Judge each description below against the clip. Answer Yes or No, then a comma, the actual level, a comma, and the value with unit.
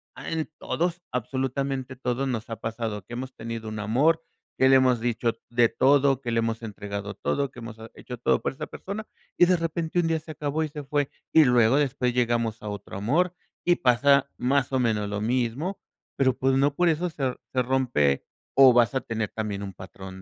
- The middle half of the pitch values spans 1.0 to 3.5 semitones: No, average, 3.9 semitones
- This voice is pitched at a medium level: No, low, 125 Hz